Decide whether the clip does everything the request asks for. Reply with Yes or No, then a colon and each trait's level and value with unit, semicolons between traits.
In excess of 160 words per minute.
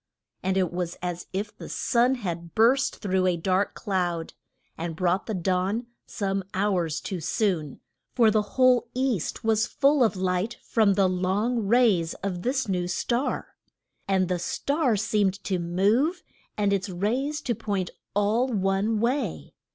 No: average, 155 wpm